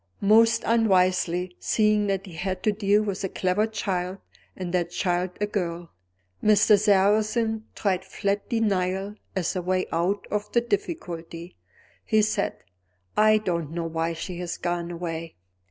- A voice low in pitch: No, high, 190 Hz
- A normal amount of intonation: Yes, average, 3.2 semitones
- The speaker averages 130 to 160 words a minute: Yes, average, 150 wpm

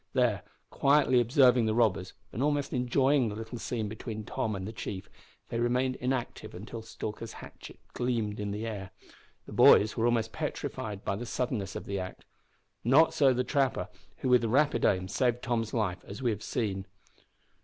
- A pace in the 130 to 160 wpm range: No, average, 175 wpm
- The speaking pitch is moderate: No, low, 115 Hz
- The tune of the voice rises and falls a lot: No, average, 3.3 semitones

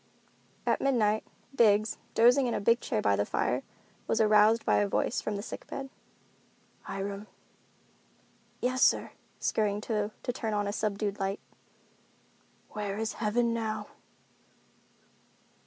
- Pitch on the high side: Yes, high, 215 Hz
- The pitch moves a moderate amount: No, narrow, 2.2 semitones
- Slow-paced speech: Yes, slow, 130 wpm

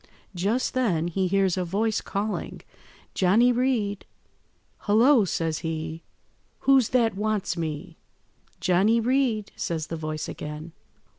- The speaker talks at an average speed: No, slow, 120 wpm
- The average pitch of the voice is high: Yes, high, 195 Hz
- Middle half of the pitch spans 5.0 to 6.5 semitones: Yes, average, 5.3 semitones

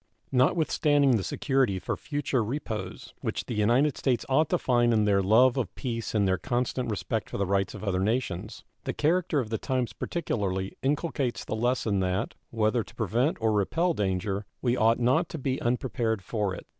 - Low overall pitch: Yes, low, 115 Hz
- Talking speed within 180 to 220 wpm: Yes, average, 185 wpm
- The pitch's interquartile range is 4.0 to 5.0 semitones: Yes, average, 4.4 semitones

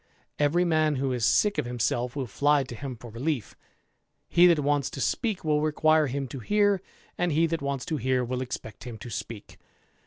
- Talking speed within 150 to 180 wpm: No, fast, 205 wpm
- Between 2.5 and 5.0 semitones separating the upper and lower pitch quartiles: Yes, average, 4.0 semitones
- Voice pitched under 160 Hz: Yes, medium, 140 Hz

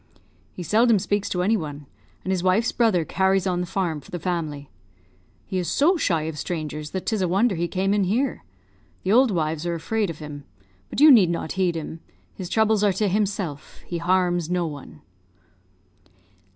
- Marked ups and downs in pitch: No, average, 3.7 semitones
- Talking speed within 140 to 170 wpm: No, average, 190 wpm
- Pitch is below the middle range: No, medium, 185 Hz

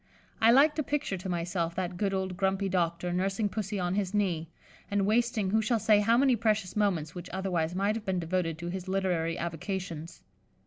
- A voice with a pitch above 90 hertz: Yes, high, 190 Hz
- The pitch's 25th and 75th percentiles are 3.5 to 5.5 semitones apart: No, average, 3.0 semitones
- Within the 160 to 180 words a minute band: No, average, 195 wpm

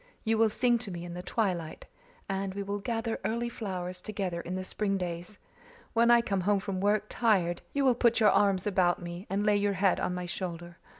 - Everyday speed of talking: No, fast, 220 wpm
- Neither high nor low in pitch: No, high, 195 Hz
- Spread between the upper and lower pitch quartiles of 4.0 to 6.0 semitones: No, average, 3.3 semitones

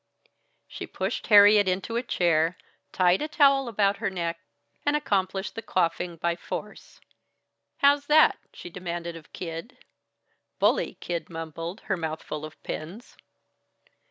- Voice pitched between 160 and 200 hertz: Yes, medium, 185 Hz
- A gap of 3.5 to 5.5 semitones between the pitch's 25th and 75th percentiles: Yes, average, 4.7 semitones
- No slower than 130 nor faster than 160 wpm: Yes, slow, 135 wpm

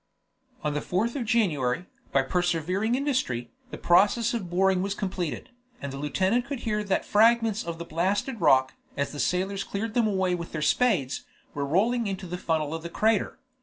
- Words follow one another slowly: No, average, 185 wpm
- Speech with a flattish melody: No, wide, 5.4 semitones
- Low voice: No, medium, 185 Hz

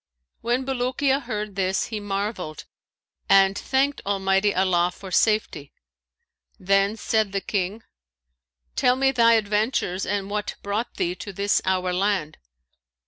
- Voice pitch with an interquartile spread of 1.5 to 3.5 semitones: Yes, average, 2.8 semitones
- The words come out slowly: Yes, slow, 130 wpm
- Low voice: No, high, 205 Hz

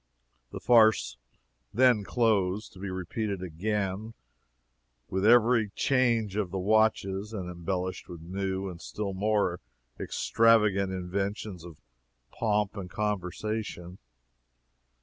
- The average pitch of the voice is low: Yes, low, 100 Hz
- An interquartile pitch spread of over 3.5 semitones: No, average, 2.8 semitones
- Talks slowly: Yes, slow, 110 wpm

